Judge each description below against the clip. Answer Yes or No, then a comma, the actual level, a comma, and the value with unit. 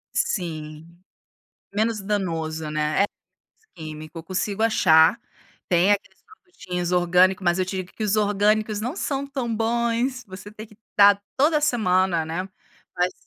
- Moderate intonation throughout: Yes, average, 4.3 semitones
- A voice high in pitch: Yes, high, 195 Hz